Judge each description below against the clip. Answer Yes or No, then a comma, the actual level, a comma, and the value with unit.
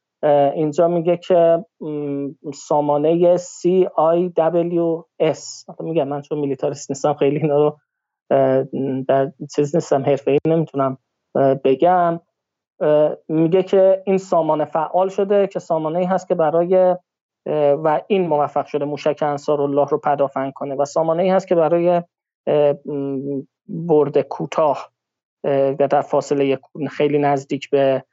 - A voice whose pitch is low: No, medium, 150 Hz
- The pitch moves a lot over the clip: No, average, 3.2 semitones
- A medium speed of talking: Yes, average, 120 wpm